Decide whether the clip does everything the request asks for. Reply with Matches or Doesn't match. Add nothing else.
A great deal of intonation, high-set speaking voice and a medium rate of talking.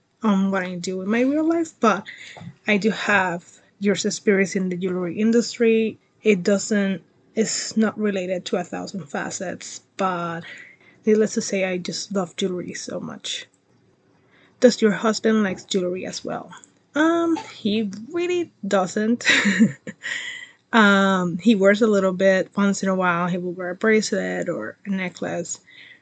Doesn't match